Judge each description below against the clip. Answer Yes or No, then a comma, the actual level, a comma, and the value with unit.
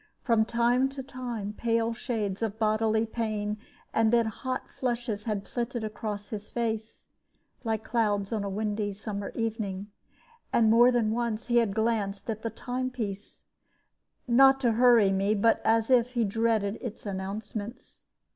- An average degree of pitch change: No, narrow, 2.3 semitones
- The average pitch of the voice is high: Yes, high, 225 Hz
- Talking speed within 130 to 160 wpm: Yes, average, 155 wpm